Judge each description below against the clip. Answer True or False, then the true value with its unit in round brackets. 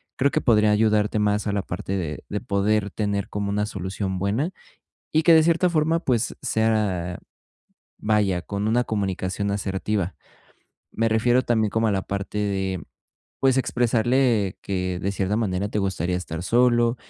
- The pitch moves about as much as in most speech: True (3.0 semitones)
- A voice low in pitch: True (105 Hz)